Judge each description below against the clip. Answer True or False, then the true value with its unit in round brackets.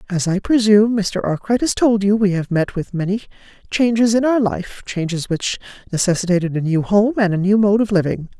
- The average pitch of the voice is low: False (200 Hz)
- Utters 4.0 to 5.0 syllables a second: False (5.5 syllables/s)